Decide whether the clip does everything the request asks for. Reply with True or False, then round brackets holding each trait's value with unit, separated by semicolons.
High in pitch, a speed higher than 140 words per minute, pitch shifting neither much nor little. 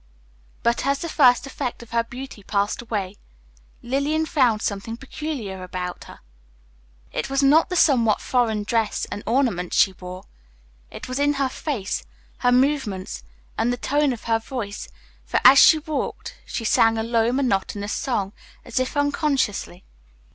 True (240 Hz; 155 wpm; 4.9 semitones)